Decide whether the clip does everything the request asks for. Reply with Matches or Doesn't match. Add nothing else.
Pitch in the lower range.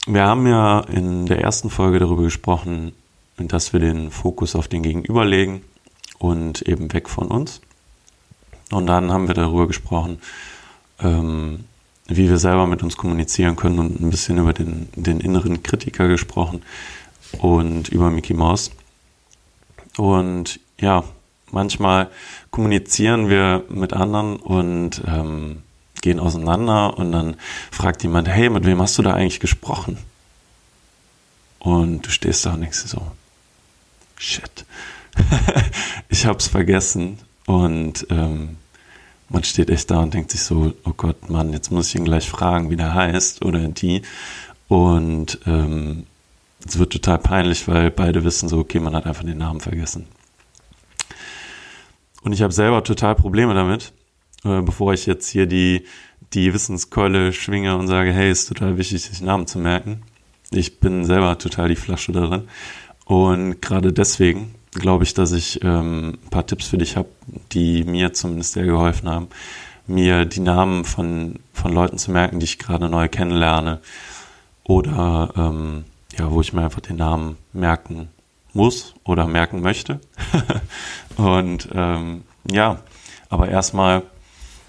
Matches